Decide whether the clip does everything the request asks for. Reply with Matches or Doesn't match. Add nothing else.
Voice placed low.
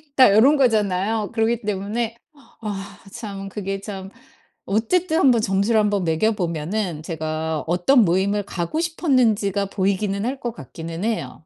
Doesn't match